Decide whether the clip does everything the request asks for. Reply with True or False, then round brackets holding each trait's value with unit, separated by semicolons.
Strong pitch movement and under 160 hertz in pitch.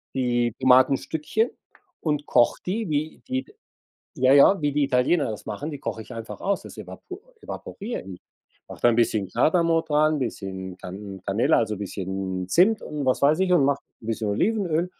True (7.1 semitones; 135 Hz)